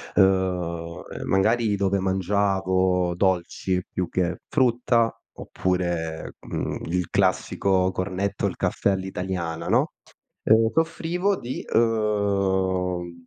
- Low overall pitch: Yes, very low, 95 Hz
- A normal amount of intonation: No, narrow, 2.1 semitones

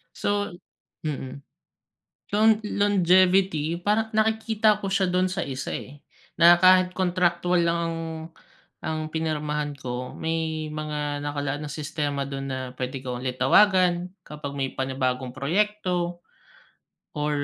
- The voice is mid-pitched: Yes, medium, 160 Hz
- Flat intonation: No, average, 4.3 semitones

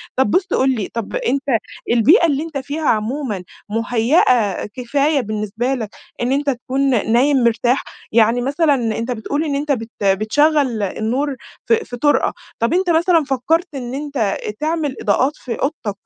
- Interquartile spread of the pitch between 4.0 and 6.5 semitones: Yes, average, 4.4 semitones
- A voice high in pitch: Yes, very high, 260 Hz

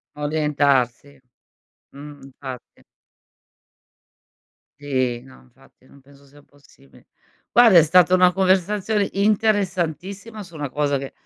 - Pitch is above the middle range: No, medium, 150 Hz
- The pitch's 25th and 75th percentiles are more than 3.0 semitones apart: Yes, average, 5.3 semitones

